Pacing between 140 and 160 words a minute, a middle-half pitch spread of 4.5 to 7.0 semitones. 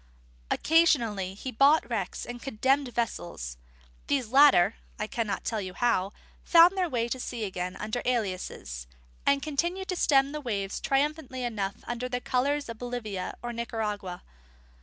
Yes: average, 150 wpm; average, 5.0 semitones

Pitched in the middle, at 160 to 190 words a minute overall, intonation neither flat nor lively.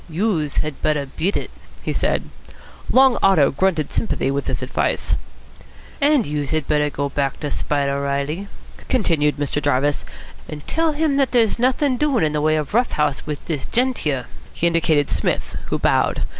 No: medium, 155 Hz; average, 175 wpm; wide, 7.8 semitones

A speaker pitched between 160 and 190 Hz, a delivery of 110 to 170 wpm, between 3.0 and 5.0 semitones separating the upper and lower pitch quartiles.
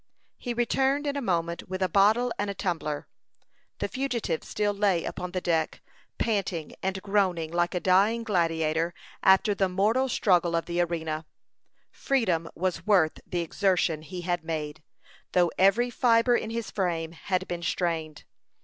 Yes: medium, 185 Hz; average, 160 wpm; average, 4.0 semitones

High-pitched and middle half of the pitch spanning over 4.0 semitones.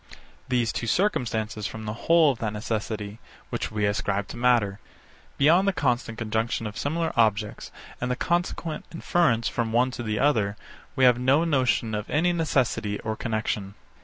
No: low, 115 Hz; average, 4.4 semitones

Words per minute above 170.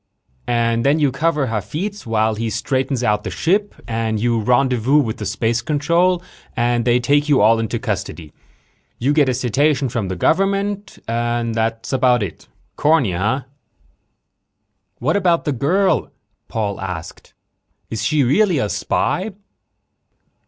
No: average, 145 wpm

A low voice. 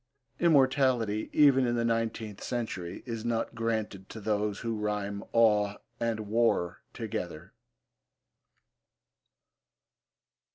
Yes: low, 110 Hz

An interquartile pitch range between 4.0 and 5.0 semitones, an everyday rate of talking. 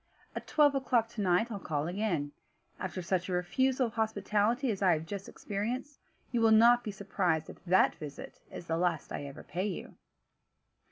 Yes: average, 4.6 semitones; average, 185 wpm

